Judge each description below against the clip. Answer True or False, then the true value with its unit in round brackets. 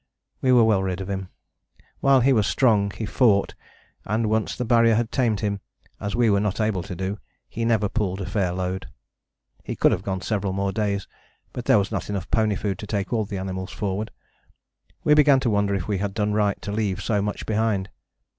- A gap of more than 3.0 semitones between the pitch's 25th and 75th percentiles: False (2.4 semitones)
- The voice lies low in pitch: True (105 Hz)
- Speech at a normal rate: False (215 wpm)